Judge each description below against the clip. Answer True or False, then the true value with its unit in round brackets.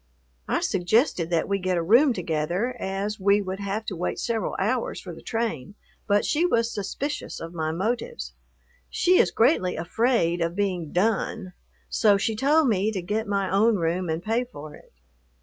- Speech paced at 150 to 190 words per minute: True (180 wpm)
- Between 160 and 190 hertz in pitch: False (200 Hz)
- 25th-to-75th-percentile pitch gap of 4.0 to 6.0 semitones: True (4.4 semitones)